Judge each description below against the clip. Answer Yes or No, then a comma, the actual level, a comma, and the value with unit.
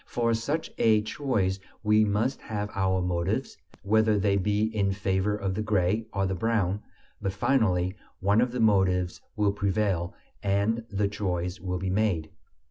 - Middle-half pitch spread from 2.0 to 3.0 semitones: Yes, narrow, 2.5 semitones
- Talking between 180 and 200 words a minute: No, average, 160 wpm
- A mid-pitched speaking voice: No, low, 100 Hz